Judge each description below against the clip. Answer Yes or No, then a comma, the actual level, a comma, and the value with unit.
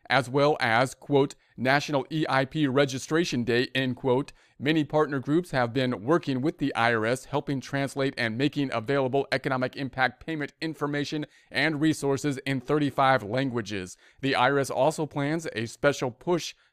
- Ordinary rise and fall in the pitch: No, narrow, 2.3 semitones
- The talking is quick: No, average, 145 wpm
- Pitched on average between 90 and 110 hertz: No, medium, 140 Hz